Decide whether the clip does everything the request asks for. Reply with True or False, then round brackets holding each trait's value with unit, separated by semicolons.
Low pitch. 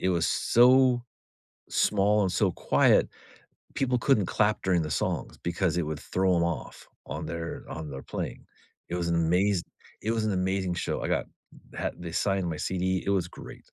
True (90 Hz)